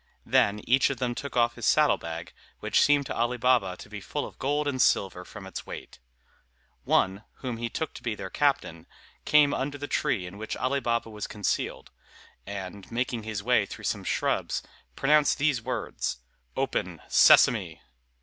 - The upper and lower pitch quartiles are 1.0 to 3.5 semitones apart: No, wide, 5.5 semitones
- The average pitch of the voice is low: Yes, low, 120 Hz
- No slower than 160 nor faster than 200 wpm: Yes, average, 180 wpm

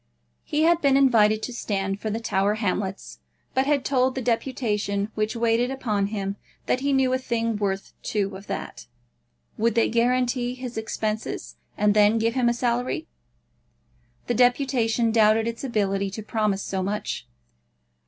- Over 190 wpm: No, average, 160 wpm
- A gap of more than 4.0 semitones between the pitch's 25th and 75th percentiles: No, average, 3.3 semitones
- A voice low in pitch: No, high, 225 Hz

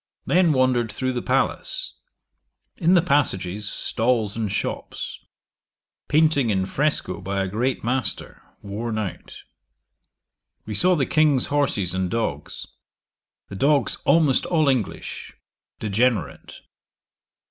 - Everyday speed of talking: No, slow, 115 wpm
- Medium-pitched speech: No, low, 120 Hz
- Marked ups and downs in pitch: Yes, wide, 5.9 semitones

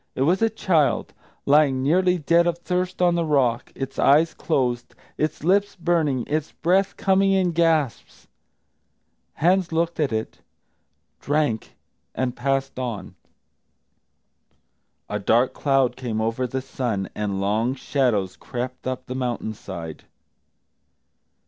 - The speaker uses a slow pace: Yes, slow, 130 wpm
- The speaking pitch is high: No, low, 135 Hz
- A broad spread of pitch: Yes, wide, 5.7 semitones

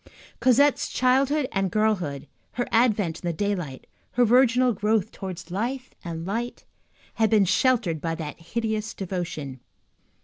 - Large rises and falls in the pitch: Yes, wide, 5.8 semitones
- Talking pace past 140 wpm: No, slow, 135 wpm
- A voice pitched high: Yes, high, 210 Hz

